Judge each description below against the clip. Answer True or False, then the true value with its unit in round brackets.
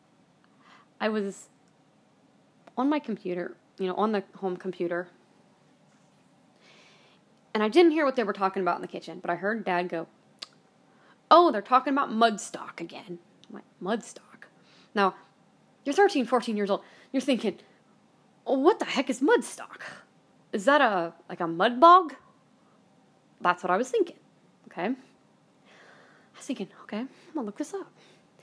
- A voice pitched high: True (215 Hz)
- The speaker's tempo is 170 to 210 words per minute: False (150 wpm)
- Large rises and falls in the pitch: True (6.4 semitones)